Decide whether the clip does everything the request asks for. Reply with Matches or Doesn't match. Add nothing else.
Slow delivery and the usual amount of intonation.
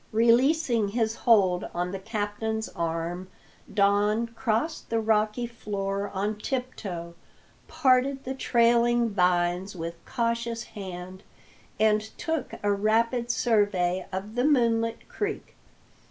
Matches